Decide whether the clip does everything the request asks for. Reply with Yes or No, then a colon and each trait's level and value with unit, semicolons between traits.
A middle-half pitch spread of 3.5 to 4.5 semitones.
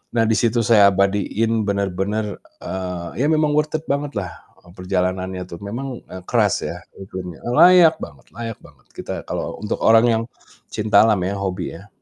Yes: average, 4.0 semitones